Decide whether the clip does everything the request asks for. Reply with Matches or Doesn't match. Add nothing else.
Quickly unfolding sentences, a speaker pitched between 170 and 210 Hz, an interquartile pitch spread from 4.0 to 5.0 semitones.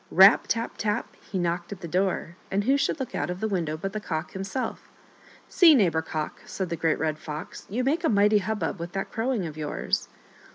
Matches